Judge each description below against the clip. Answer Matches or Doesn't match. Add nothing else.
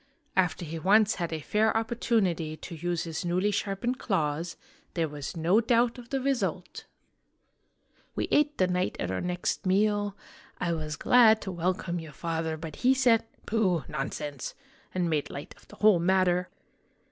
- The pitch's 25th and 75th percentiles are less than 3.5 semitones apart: Doesn't match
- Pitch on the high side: Doesn't match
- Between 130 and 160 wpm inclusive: Doesn't match